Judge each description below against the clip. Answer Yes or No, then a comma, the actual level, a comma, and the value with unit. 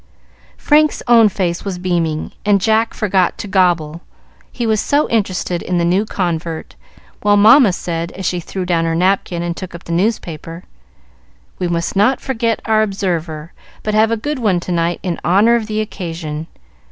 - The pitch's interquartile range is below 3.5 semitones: No, average, 4.1 semitones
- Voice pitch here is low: No, medium, 185 Hz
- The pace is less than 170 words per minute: No, average, 175 wpm